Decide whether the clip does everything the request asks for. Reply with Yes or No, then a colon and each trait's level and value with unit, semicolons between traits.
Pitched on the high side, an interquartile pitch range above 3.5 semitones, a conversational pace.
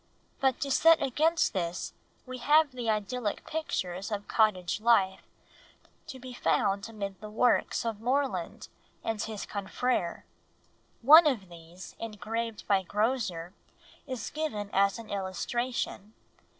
No: high, 220 Hz; average, 4.4 semitones; slow, 125 wpm